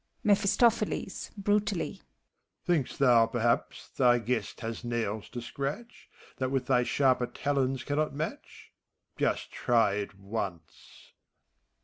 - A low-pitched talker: Yes, low, 125 Hz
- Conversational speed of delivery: No, slow, 115 wpm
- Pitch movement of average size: Yes, average, 4.6 semitones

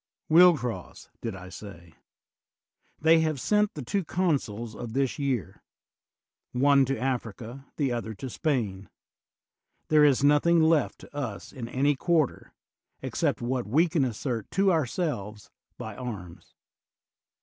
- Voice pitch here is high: No, low, 130 Hz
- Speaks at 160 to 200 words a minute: No, average, 140 wpm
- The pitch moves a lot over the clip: Yes, wide, 5.7 semitones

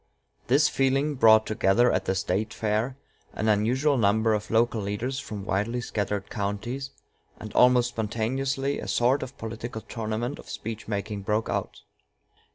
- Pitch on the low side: Yes, low, 110 Hz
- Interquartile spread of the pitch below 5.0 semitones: Yes, average, 3.0 semitones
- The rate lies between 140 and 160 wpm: Yes, average, 150 wpm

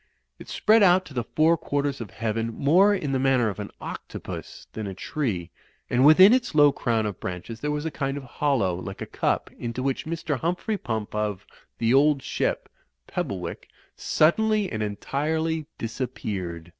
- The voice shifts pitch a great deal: Yes, wide, 6.2 semitones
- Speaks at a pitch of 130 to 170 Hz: Yes, low, 135 Hz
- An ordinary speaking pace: Yes, average, 180 wpm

